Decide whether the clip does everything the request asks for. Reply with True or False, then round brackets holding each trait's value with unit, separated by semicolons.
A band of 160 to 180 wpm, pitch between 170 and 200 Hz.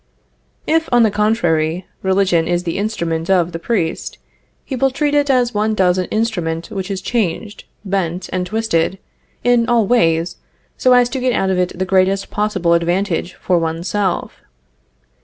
True (170 wpm; 190 Hz)